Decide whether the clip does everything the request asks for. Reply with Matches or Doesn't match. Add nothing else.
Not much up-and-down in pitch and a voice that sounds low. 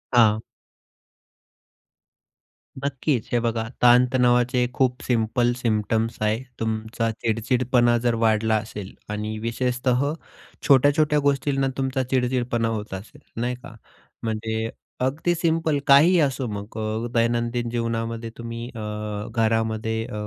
Matches